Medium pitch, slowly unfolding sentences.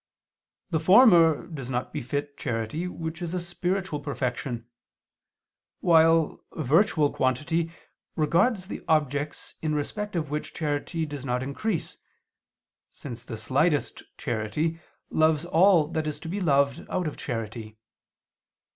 Yes: medium, 155 Hz; slow, 125 wpm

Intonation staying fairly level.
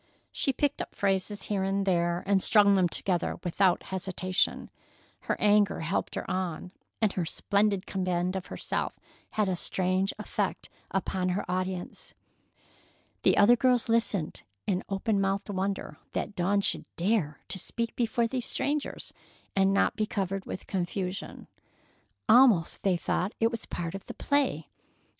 Yes: narrow, 2.3 semitones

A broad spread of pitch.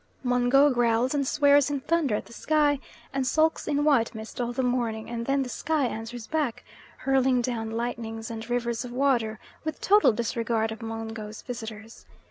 No: average, 3.5 semitones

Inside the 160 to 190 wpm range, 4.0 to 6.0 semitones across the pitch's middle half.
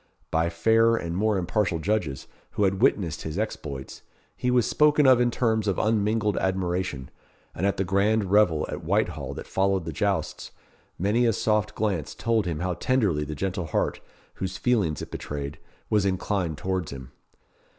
Yes: average, 170 wpm; average, 4.5 semitones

